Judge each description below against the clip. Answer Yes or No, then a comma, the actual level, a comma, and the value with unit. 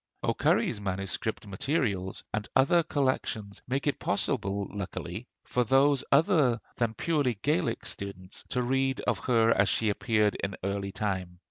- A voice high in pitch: No, low, 110 Hz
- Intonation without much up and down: No, average, 5.2 semitones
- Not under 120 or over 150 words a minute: Yes, slow, 135 wpm